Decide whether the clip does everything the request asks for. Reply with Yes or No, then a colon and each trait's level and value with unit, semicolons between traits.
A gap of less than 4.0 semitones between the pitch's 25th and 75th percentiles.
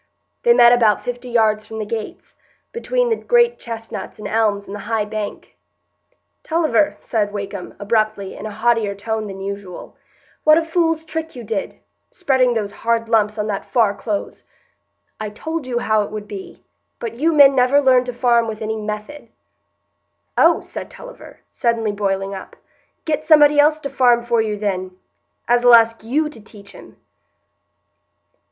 No: average, 4.6 semitones